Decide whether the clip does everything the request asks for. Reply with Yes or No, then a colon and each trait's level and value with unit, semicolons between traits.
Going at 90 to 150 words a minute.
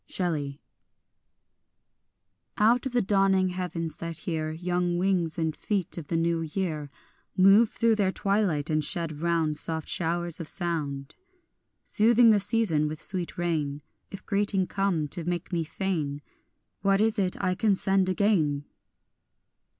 Yes: average, 145 wpm